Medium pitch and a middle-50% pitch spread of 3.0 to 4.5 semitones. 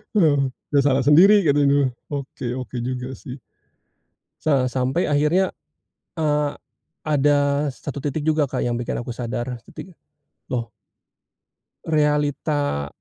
No: medium, 145 Hz; narrow, 2.6 semitones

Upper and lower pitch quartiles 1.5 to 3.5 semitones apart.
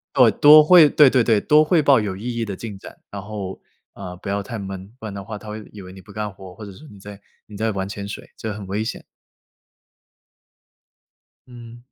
Yes: average, 3.0 semitones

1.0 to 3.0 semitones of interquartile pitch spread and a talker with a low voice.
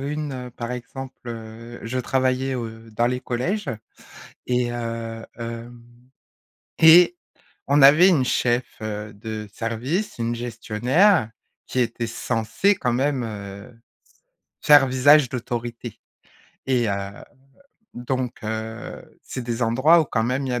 Yes: narrow, 2.6 semitones; low, 120 Hz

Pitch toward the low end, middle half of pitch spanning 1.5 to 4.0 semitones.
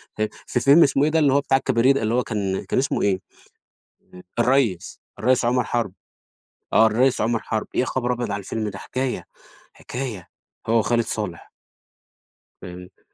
Yes: low, 120 Hz; average, 3.5 semitones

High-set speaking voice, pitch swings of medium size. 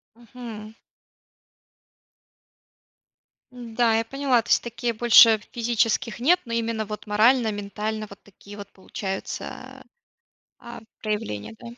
No: high, 225 Hz; narrow, 2.1 semitones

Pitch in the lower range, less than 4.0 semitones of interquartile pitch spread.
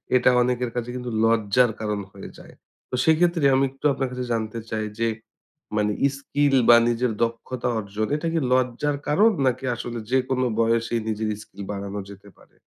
Yes: low, 120 Hz; average, 3.1 semitones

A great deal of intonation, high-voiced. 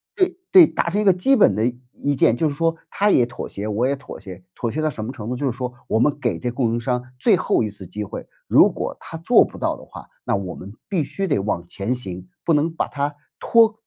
No: wide, 7.3 semitones; low, 130 Hz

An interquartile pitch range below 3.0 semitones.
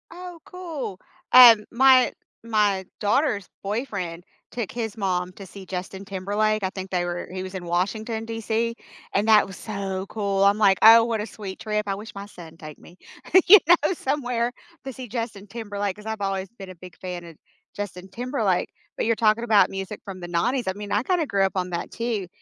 No: average, 3.4 semitones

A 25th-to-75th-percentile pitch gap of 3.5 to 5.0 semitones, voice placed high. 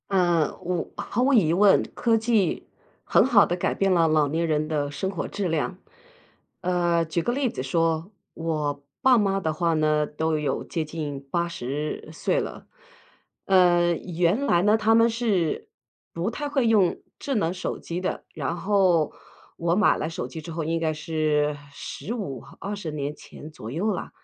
No: average, 4.2 semitones; medium, 170 Hz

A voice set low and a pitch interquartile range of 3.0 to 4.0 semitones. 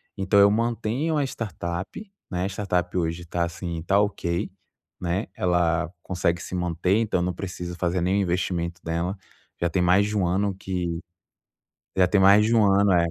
No: very low, 90 Hz; narrow, 2.6 semitones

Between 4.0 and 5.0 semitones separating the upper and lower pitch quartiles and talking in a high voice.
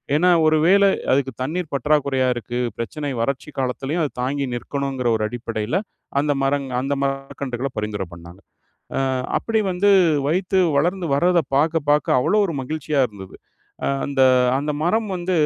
No: average, 4.5 semitones; medium, 140 Hz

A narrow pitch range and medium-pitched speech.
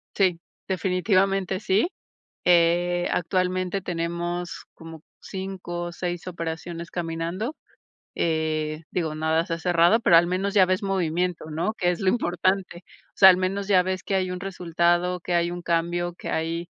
Yes: narrow, 1.8 semitones; medium, 175 Hz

